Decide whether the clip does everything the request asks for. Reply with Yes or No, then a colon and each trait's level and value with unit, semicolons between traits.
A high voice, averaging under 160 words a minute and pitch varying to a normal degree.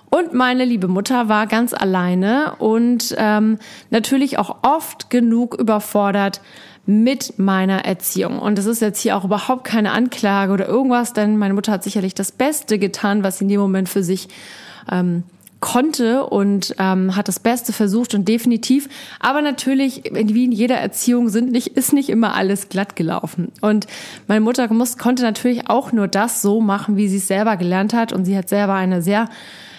No: high, 215 Hz; average, 180 wpm; average, 3.5 semitones